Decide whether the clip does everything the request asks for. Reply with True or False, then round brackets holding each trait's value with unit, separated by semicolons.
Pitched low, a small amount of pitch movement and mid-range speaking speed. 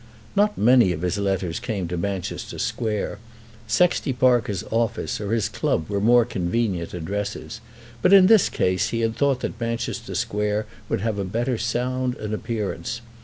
False (110 Hz; 3.5 semitones; 165 wpm)